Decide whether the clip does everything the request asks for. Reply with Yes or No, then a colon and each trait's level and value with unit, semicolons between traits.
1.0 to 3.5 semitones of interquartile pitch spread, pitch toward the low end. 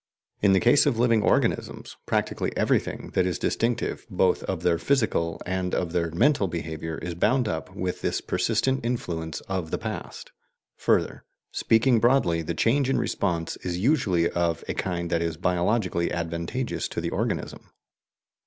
No: wide, 5.5 semitones; very low, 90 Hz